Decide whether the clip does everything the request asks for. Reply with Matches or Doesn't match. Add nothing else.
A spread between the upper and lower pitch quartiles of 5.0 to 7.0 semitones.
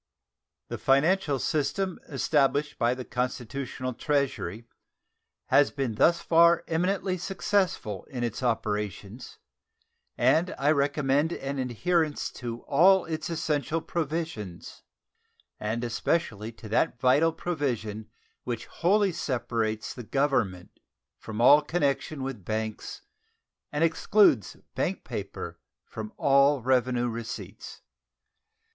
Matches